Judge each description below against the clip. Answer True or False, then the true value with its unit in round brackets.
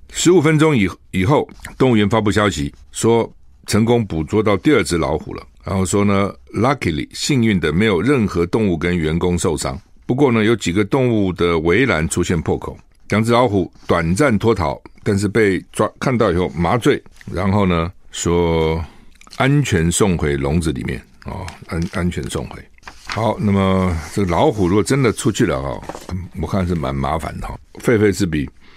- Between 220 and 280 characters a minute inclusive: True (265 characters per minute)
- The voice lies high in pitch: False (95 Hz)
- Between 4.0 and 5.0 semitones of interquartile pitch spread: True (4.4 semitones)